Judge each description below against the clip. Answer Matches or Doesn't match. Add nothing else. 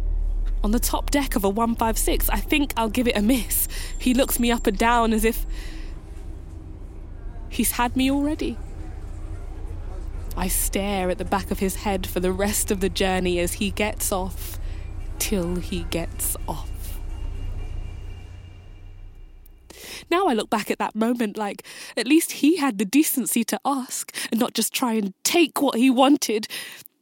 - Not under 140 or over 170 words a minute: Matches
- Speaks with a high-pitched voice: Matches